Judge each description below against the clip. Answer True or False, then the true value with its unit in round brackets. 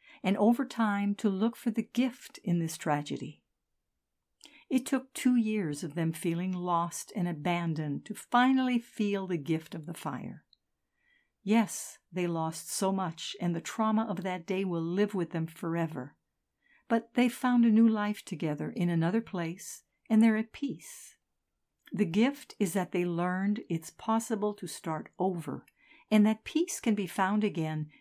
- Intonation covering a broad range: False (5.0 semitones)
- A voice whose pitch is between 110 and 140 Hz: False (200 Hz)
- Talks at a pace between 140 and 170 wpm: True (165 wpm)